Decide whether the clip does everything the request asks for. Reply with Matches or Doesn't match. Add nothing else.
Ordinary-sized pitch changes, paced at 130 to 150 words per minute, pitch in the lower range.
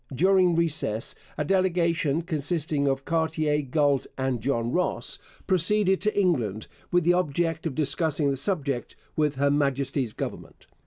Doesn't match